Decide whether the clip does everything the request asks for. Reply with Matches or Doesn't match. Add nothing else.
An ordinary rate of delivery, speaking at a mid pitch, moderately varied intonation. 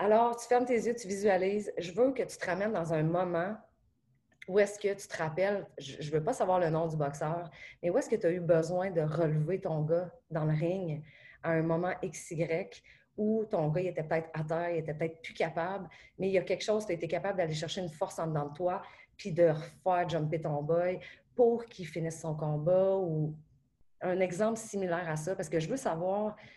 Doesn't match